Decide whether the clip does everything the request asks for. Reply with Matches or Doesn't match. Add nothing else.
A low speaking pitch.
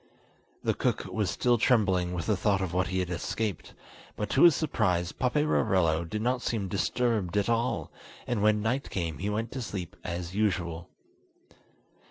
Matches